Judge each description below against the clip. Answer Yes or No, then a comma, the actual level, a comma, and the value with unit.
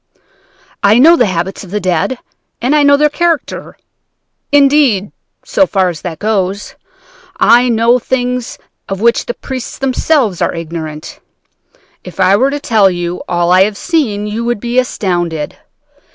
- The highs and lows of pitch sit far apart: Yes, wide, 5.9 semitones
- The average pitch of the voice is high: Yes, high, 215 Hz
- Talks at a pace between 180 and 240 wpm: No, average, 155 wpm